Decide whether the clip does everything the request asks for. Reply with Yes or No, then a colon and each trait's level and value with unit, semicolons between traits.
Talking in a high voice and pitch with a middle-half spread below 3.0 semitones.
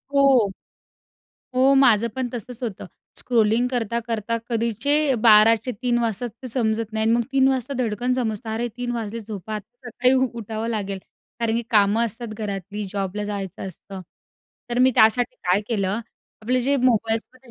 Yes: high, 230 Hz; narrow, 2.6 semitones